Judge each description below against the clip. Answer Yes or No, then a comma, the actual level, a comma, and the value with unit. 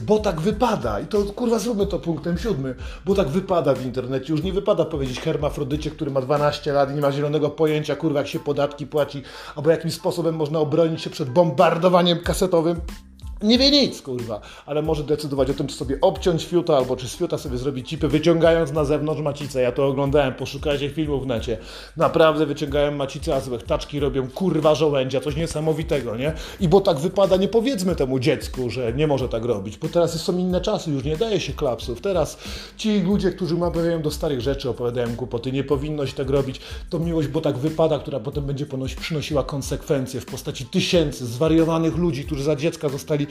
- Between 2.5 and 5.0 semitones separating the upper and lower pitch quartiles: Yes, average, 3.4 semitones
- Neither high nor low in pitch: Yes, medium, 155 Hz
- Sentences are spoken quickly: Yes, fast, 195 wpm